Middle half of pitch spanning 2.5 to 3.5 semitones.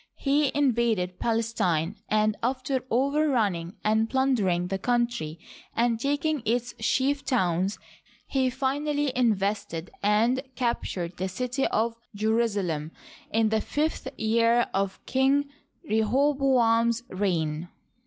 No: average, 4.9 semitones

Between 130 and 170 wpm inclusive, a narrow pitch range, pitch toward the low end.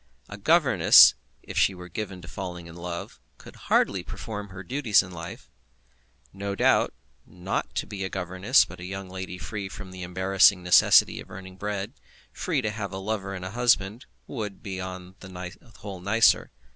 No: average, 180 wpm; narrow, 2.1 semitones; very low, 95 Hz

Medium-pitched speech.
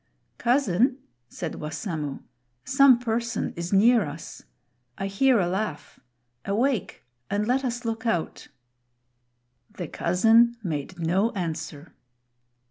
No: high, 205 Hz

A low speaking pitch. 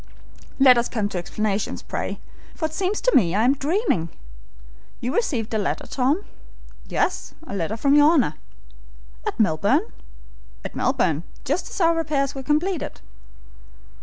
No: very high, 270 Hz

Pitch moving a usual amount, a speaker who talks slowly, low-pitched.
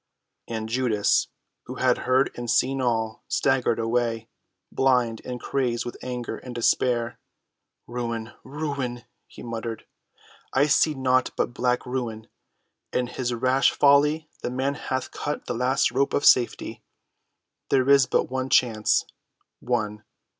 No: narrow, 2.1 semitones; slow, 130 wpm; low, 125 Hz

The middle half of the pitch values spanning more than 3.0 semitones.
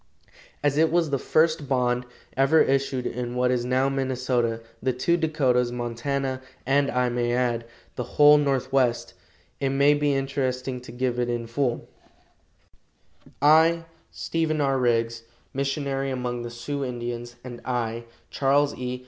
No: narrow, 2.4 semitones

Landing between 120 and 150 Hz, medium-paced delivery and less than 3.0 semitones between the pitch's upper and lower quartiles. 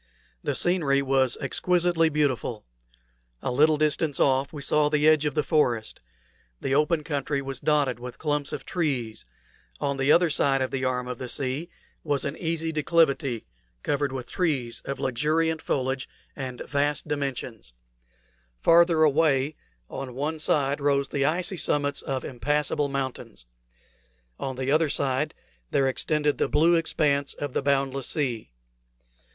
Yes: medium, 140 Hz; average, 150 wpm; narrow, 2.6 semitones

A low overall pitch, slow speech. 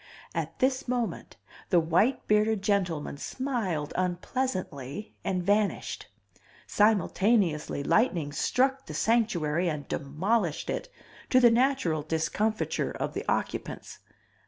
No: high, 200 Hz; slow, 110 wpm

